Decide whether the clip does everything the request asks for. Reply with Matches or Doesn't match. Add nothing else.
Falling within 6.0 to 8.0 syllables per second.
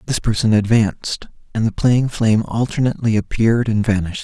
Matches